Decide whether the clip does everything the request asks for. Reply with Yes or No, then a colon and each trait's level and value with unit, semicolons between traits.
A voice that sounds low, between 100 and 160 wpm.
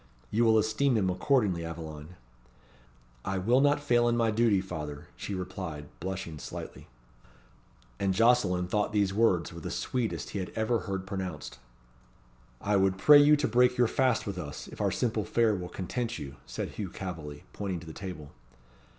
No: very low, 95 Hz; average, 175 wpm